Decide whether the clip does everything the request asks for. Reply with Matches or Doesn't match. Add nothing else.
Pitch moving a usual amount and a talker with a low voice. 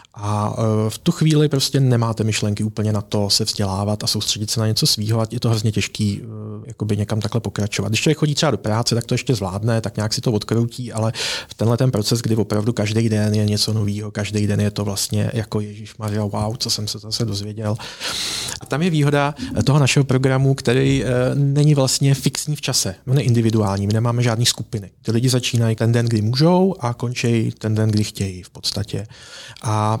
Matches